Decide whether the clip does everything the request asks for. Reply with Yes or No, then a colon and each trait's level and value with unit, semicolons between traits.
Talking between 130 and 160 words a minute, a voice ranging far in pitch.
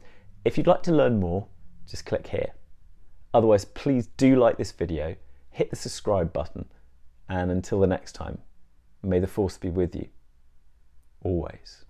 Yes: average, 155 wpm; wide, 6.3 semitones